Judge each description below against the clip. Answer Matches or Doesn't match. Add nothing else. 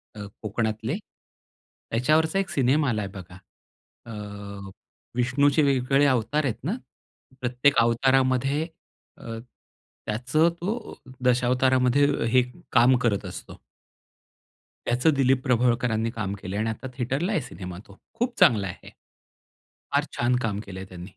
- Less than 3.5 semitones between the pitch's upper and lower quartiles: Doesn't match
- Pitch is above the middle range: Doesn't match